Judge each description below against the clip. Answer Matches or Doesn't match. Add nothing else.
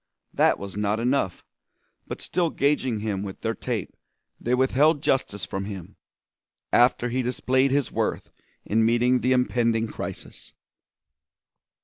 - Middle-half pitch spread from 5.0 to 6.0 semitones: Doesn't match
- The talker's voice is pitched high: Doesn't match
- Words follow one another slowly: Matches